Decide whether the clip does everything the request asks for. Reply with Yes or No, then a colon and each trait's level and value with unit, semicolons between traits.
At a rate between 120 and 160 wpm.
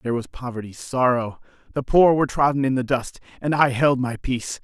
No: fast, 205 wpm